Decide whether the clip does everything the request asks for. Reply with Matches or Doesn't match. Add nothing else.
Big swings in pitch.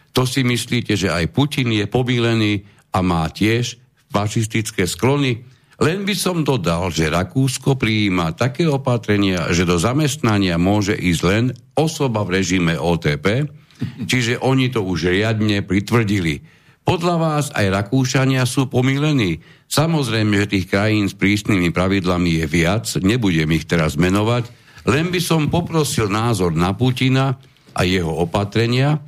Matches